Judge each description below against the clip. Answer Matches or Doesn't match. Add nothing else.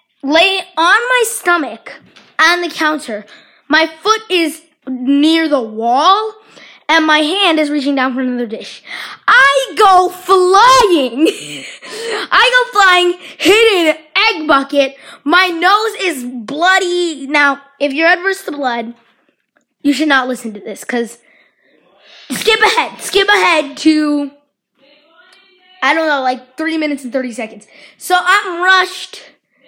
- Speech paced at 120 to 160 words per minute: Matches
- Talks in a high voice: Matches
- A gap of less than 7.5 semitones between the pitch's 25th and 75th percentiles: Matches